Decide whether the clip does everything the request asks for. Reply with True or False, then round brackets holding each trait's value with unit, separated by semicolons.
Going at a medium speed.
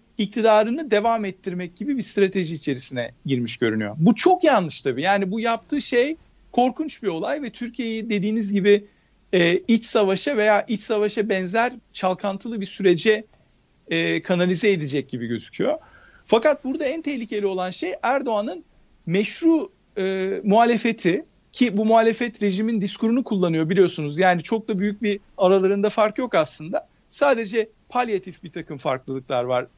False (145 wpm)